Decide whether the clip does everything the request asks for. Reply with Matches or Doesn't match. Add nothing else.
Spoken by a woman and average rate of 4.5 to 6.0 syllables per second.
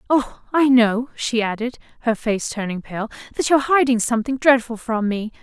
Matches